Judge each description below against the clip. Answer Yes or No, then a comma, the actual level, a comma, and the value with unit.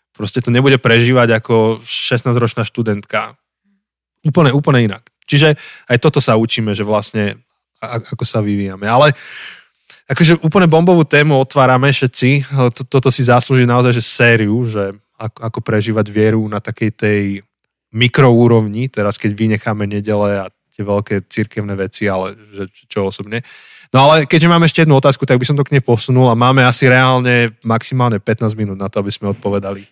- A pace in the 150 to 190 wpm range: Yes, average, 160 wpm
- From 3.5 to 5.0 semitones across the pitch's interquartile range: Yes, average, 3.8 semitones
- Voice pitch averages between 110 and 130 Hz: Yes, low, 120 Hz